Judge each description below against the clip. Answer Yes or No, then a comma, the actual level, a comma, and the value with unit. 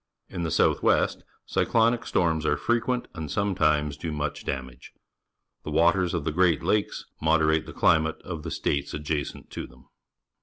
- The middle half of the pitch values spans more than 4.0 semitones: No, average, 3.2 semitones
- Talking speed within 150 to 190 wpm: Yes, average, 165 wpm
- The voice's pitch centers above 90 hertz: No, very low, 80 Hz